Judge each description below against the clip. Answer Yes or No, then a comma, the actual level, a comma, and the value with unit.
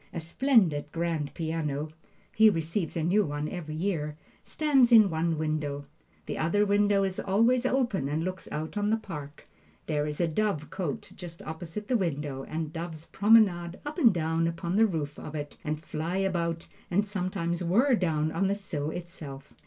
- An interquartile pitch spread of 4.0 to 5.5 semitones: Yes, average, 4.6 semitones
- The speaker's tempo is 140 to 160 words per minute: No, average, 175 wpm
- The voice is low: No, medium, 170 Hz